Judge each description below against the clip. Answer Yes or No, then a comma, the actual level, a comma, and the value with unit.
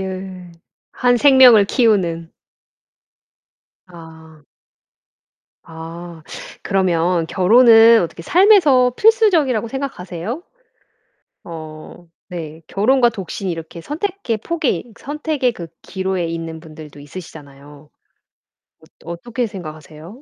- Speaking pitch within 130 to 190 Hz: Yes, medium, 185 Hz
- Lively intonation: Yes, wide, 7.1 semitones